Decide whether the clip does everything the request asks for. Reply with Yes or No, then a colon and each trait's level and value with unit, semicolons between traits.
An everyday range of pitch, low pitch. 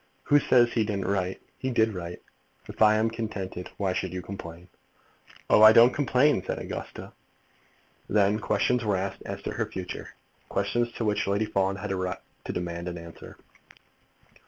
Yes: average, 3.4 semitones; low, 100 Hz